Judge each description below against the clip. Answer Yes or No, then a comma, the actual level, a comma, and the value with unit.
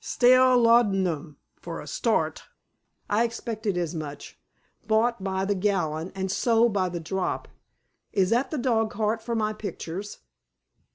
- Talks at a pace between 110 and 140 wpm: Yes, slow, 135 wpm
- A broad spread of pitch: No, average, 3.8 semitones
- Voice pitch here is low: No, high, 205 Hz